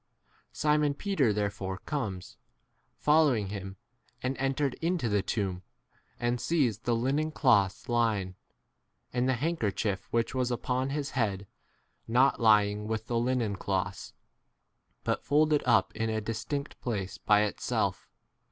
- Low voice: Yes, low, 115 Hz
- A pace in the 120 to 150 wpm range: Yes, average, 140 wpm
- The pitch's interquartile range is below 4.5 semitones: No, average, 4.9 semitones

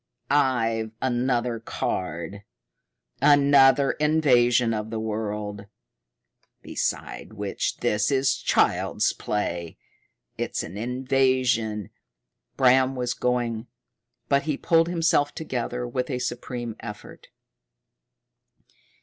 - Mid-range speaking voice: No, low, 125 Hz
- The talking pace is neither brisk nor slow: No, slow, 95 wpm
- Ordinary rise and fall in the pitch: Yes, average, 3.4 semitones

